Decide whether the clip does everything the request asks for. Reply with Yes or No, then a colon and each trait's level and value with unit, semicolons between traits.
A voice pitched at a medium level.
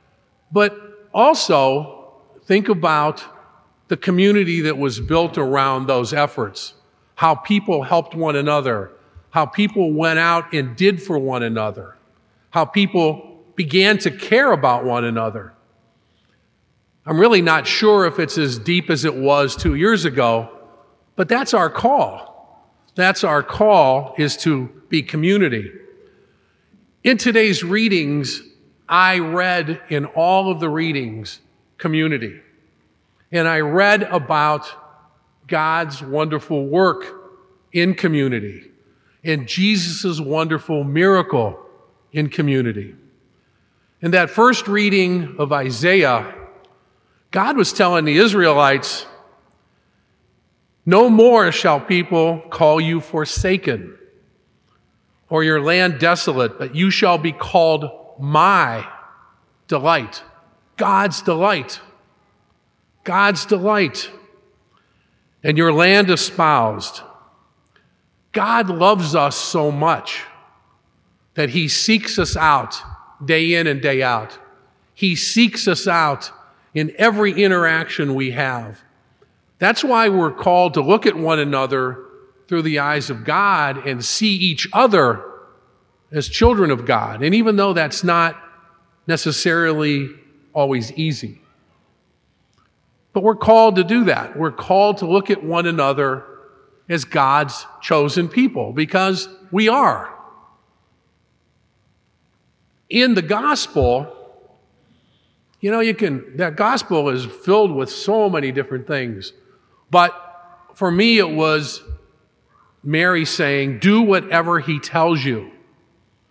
Yes: medium, 165 Hz